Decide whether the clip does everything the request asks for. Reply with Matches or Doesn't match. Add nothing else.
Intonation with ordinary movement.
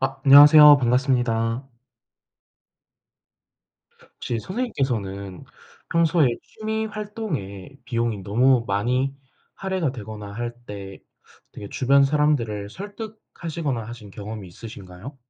Doesn't match